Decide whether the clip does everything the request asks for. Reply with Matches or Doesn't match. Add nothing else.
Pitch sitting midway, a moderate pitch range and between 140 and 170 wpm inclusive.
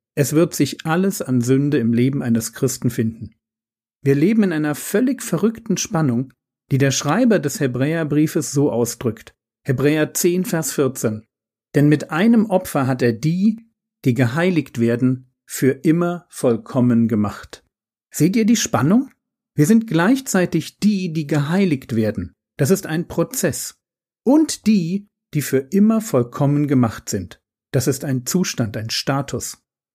Doesn't match